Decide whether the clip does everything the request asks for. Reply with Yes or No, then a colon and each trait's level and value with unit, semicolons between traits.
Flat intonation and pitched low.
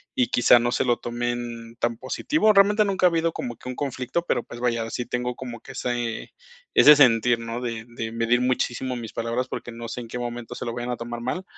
Yes: narrow, 1.5 semitones; low, 120 Hz